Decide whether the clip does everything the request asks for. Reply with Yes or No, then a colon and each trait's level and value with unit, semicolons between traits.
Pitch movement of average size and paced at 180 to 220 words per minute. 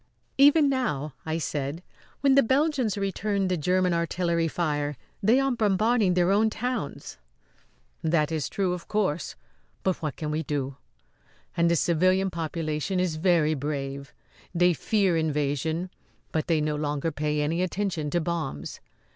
No: average, 4.4 semitones; average, 145 wpm